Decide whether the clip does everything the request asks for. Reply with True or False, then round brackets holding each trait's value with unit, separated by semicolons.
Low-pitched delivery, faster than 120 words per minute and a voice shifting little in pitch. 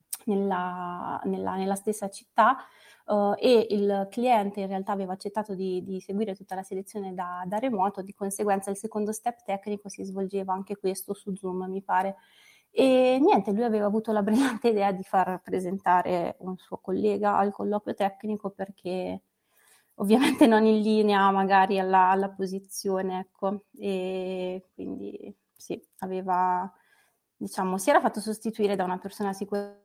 False (195 Hz; 155 wpm; 2.0 semitones)